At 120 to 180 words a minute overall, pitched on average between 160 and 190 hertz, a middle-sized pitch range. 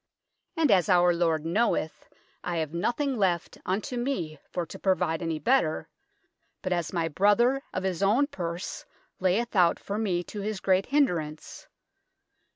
Yes: average, 160 wpm; medium, 185 Hz; average, 4.3 semitones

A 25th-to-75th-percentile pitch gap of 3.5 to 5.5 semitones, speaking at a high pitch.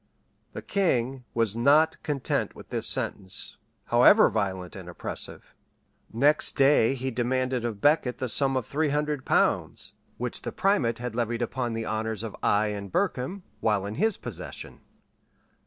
No: average, 4.1 semitones; low, 125 Hz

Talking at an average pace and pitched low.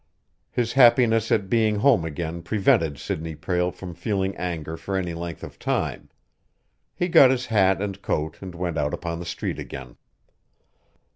Yes: average, 160 wpm; very low, 90 Hz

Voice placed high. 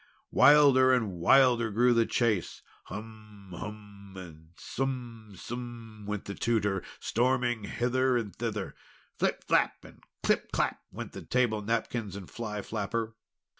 No: low, 115 Hz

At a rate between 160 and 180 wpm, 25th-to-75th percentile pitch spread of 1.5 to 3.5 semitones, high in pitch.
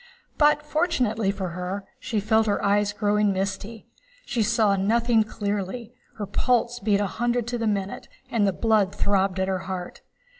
Yes: average, 165 wpm; average, 2.9 semitones; high, 210 Hz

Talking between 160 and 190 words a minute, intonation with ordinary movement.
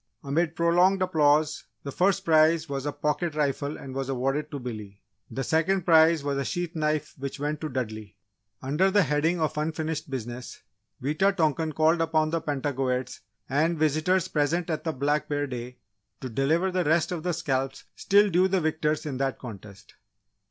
Yes: average, 175 wpm; average, 3.3 semitones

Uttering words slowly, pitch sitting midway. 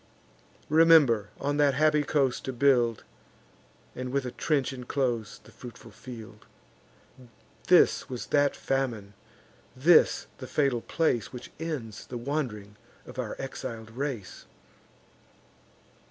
No: slow, 115 wpm; low, 130 Hz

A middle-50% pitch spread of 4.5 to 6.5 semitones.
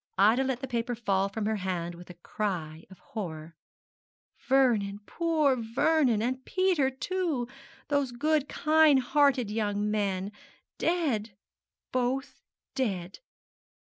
Yes: wide, 5.5 semitones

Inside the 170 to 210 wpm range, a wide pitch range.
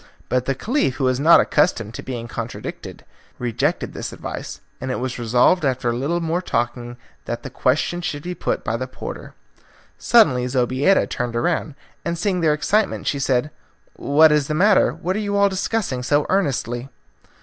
Yes: average, 180 wpm; wide, 6.0 semitones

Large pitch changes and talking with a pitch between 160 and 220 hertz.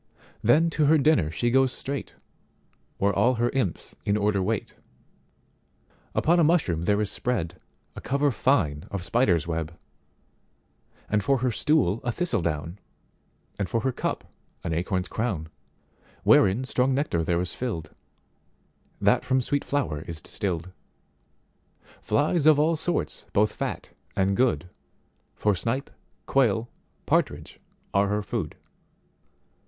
No: wide, 7.0 semitones; low, 105 Hz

